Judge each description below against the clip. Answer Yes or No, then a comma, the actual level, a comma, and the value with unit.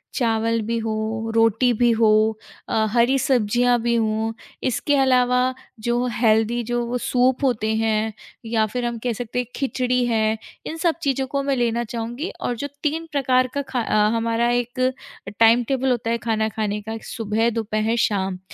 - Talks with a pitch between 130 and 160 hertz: No, high, 235 Hz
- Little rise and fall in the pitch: Yes, narrow, 2.1 semitones